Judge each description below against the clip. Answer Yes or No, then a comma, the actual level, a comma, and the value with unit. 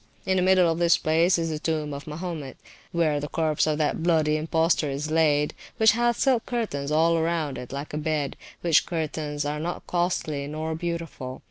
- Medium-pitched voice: Yes, medium, 160 Hz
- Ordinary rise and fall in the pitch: No, narrow, 2.3 semitones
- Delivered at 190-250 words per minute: Yes, average, 195 wpm